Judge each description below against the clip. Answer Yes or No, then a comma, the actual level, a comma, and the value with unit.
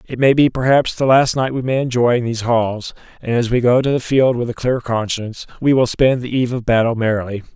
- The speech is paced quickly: Yes, fast, 255 wpm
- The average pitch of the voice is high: No, low, 120 Hz